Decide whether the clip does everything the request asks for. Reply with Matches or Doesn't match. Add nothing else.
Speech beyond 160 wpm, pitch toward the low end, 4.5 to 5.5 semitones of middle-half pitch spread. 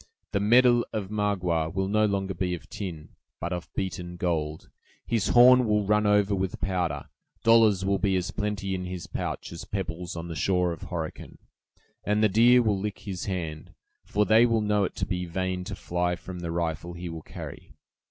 Doesn't match